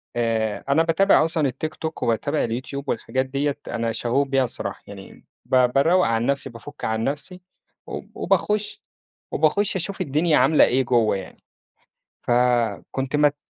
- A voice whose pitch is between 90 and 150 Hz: Yes, medium, 140 Hz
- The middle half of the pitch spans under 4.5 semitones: No, average, 5.0 semitones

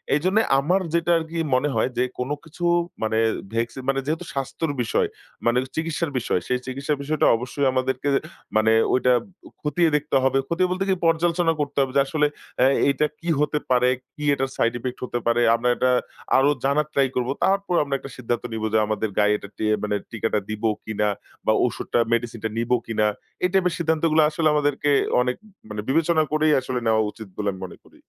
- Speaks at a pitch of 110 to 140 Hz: Yes, low, 135 Hz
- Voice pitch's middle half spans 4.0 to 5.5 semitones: Yes, average, 5.0 semitones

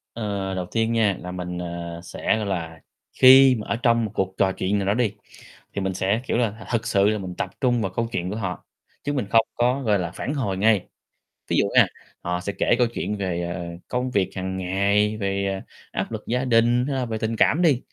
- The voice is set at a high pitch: No, low, 105 Hz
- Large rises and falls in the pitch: No, average, 3.8 semitones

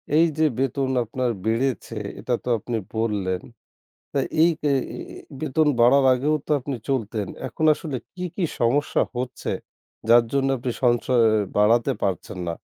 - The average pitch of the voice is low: Yes, low, 125 Hz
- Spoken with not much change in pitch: No, average, 3.2 semitones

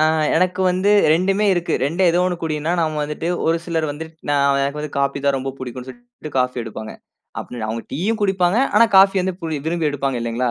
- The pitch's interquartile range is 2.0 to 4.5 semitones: No, average, 4.9 semitones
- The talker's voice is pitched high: No, medium, 155 Hz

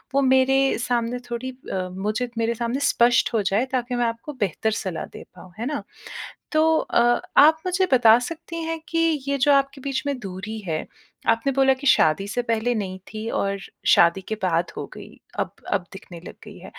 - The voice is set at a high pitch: Yes, high, 235 Hz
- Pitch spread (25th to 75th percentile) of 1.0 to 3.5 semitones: No, average, 5.0 semitones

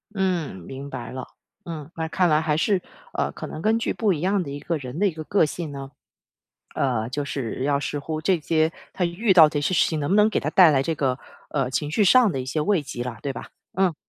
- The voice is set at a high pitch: No, medium, 155 Hz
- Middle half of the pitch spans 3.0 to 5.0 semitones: Yes, average, 4.5 semitones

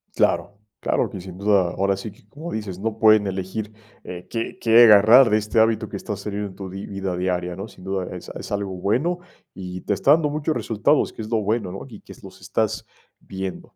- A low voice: Yes, low, 100 Hz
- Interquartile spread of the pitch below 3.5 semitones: Yes, average, 2.8 semitones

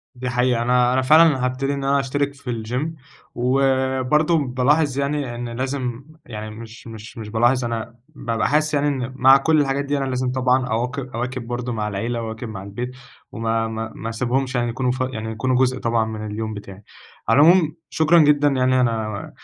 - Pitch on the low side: Yes, low, 125 Hz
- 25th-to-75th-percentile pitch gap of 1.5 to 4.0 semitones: Yes, average, 3.0 semitones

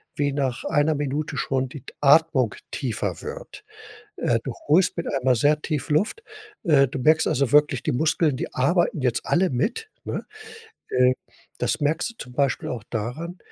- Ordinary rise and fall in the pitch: Yes, average, 3.9 semitones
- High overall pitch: No, medium, 145 Hz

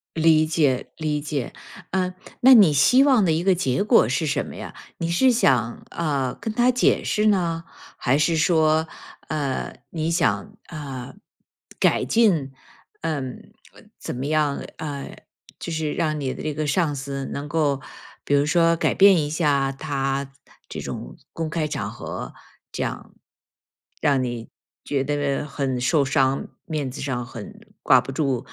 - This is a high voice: No, medium, 150 Hz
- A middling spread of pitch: Yes, average, 3.4 semitones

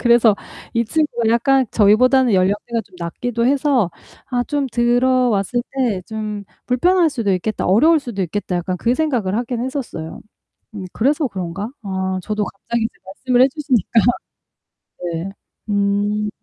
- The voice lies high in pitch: Yes, high, 230 Hz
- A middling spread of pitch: Yes, average, 4.1 semitones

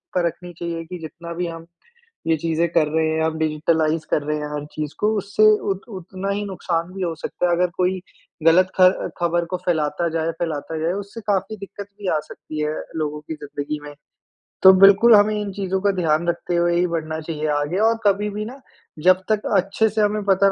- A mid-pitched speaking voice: Yes, medium, 175 Hz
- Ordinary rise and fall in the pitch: Yes, average, 3.6 semitones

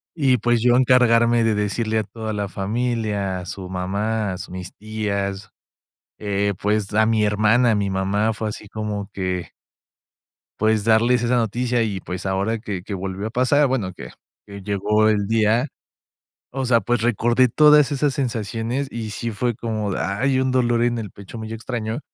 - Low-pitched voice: Yes, low, 110 Hz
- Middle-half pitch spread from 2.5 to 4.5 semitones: Yes, average, 2.8 semitones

